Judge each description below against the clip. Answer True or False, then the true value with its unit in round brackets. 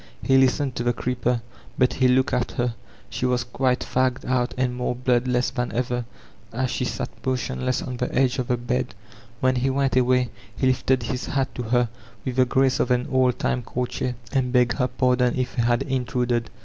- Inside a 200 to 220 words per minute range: True (205 wpm)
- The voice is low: True (125 Hz)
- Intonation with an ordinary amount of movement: False (0.9 semitones)